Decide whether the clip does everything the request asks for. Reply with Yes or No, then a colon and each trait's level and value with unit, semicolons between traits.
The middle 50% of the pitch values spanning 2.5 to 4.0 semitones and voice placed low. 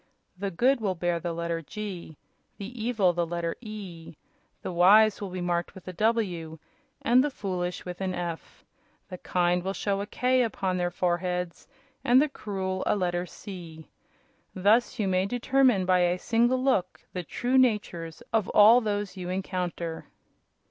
No: average, 3.5 semitones; medium, 185 Hz